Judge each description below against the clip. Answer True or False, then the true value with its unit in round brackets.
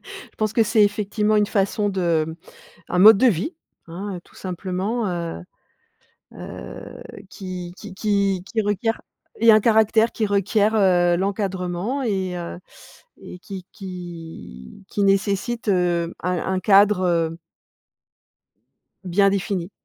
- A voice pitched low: False (195 Hz)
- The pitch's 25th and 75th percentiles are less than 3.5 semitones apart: True (2.9 semitones)